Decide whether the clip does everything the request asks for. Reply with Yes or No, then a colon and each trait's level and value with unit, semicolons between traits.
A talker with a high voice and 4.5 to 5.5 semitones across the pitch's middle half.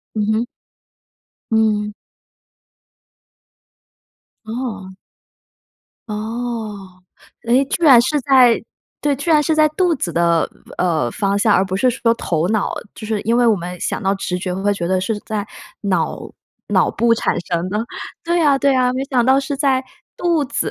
Yes: high, 220 Hz; average, 5.2 semitones